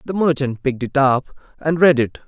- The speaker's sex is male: Yes, male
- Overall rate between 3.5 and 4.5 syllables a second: No, 5.8 syllables/s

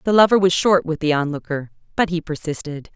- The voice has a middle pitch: Yes, medium, 165 Hz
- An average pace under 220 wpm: Yes, fast, 205 wpm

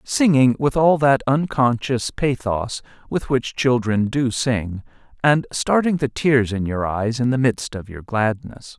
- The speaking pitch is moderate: No, low, 125 Hz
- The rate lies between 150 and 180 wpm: Yes, average, 165 wpm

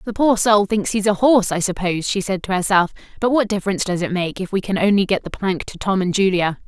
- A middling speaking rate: No, fast, 270 wpm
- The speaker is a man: No, female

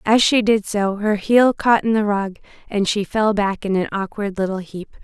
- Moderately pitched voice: No, high, 205 Hz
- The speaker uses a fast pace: Yes, fast, 225 wpm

